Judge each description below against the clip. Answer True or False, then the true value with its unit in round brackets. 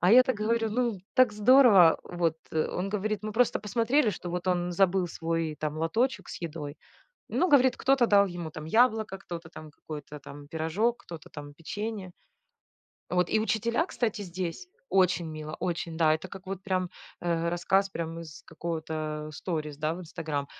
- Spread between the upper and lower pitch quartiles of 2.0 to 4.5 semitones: False (5.0 semitones)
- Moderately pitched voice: True (180 Hz)